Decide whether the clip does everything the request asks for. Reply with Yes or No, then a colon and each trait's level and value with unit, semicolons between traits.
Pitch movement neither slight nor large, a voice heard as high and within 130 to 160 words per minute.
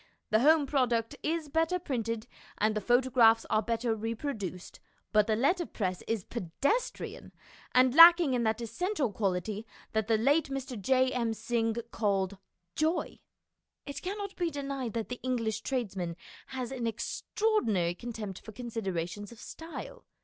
Yes: average, 4.3 semitones; high, 235 Hz; average, 145 wpm